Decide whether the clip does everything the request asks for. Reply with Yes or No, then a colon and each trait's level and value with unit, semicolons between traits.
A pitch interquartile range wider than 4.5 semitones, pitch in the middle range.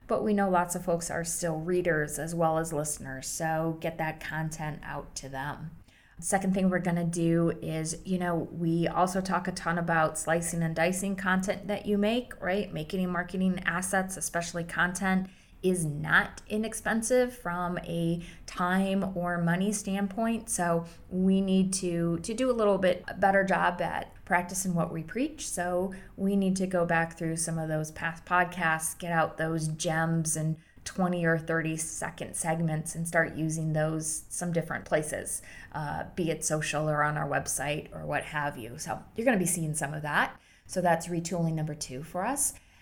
No: narrow, 2.6 semitones; medium, 170 Hz